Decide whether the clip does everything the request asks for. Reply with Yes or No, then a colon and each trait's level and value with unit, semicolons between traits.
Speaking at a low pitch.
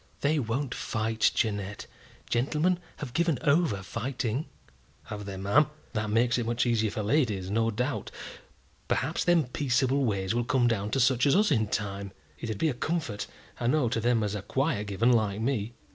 Yes: low, 120 Hz